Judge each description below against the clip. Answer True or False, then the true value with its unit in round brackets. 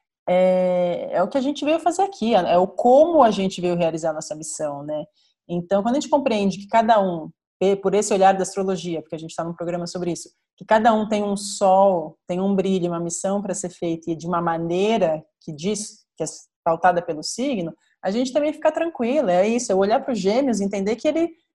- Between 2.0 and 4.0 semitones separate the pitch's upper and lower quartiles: False (4.8 semitones)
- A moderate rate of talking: False (225 wpm)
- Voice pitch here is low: False (190 Hz)